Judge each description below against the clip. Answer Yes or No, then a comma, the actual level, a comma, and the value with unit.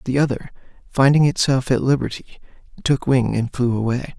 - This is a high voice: No, low, 130 Hz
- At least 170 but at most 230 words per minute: No, average, 160 wpm